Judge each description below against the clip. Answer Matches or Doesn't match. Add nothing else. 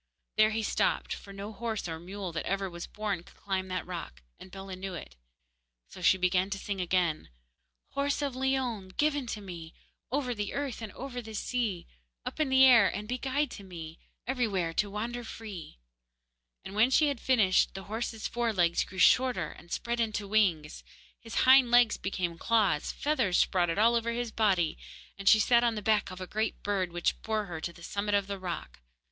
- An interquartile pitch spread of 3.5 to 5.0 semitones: Matches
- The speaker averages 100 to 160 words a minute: Doesn't match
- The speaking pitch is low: Doesn't match